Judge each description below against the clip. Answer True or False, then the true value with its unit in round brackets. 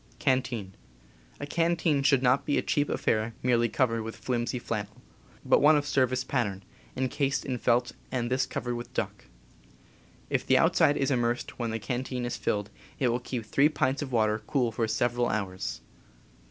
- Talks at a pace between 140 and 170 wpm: False (180 wpm)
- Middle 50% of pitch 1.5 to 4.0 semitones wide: True (2.9 semitones)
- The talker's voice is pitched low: True (125 Hz)